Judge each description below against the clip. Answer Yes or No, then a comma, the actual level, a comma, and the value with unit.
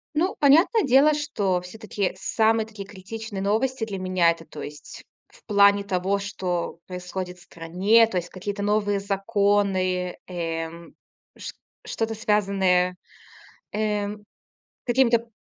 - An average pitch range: Yes, average, 3.4 semitones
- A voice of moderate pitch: No, high, 200 Hz